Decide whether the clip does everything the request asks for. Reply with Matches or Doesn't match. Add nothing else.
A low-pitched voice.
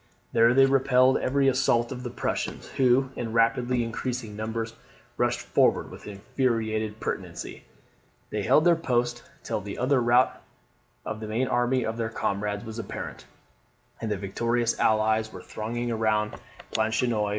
Matches